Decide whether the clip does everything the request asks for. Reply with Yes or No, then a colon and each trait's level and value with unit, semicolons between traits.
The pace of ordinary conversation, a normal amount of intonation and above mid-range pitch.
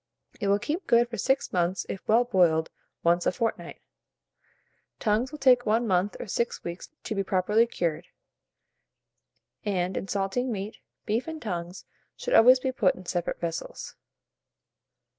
Yes: average, 155 wpm; average, 4.9 semitones; high, 205 Hz